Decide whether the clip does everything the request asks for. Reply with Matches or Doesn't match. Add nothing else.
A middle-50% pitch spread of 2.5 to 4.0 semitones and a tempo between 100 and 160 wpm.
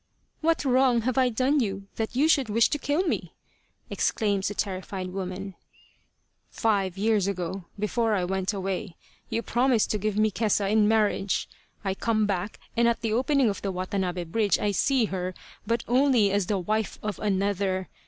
Doesn't match